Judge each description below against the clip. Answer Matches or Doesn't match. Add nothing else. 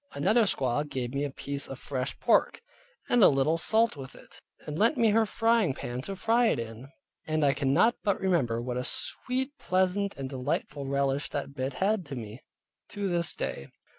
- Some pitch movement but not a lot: Doesn't match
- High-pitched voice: Doesn't match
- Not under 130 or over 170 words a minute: Doesn't match